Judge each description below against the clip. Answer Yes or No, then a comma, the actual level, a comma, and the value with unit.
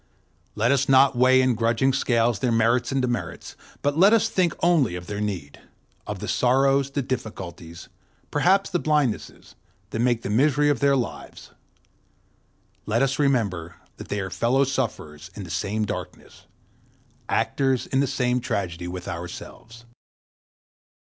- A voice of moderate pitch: No, low, 125 Hz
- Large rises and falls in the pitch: No, average, 4.7 semitones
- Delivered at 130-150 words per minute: Yes, average, 145 wpm